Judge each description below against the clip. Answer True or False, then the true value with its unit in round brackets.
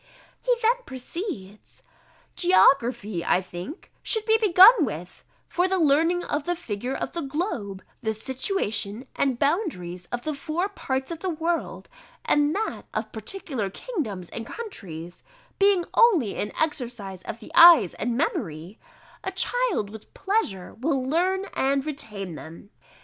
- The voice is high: True (280 Hz)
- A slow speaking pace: False (145 wpm)